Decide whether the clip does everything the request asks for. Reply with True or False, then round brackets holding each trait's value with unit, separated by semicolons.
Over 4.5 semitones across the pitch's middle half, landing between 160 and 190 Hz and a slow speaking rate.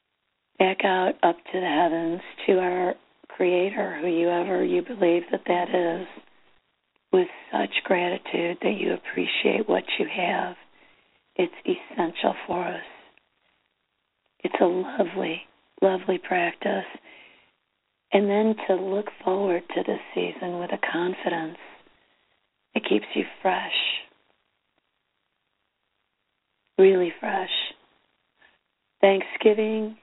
False (3.3 semitones; 185 Hz; 100 wpm)